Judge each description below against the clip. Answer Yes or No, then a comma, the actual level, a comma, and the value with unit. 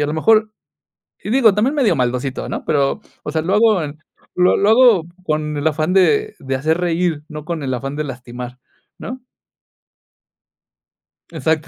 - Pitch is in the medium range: Yes, medium, 160 Hz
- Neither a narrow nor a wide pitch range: No, wide, 6.1 semitones